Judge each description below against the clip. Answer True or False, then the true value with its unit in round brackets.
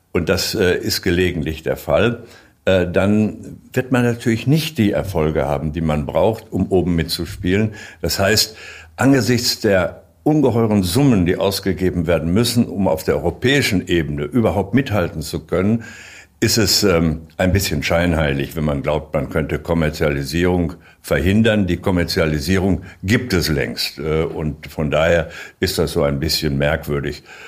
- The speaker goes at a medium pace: True (140 wpm)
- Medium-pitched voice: False (90 Hz)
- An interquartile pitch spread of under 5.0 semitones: False (5.5 semitones)